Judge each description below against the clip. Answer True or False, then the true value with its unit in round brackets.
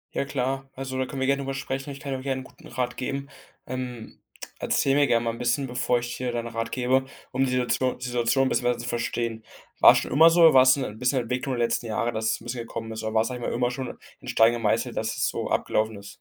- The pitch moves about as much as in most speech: False (2.3 semitones)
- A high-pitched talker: False (125 Hz)